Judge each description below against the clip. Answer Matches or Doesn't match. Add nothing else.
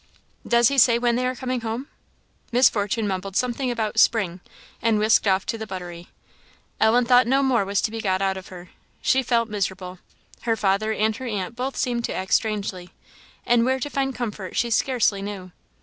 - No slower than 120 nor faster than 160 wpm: Doesn't match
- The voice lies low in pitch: Doesn't match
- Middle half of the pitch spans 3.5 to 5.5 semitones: Matches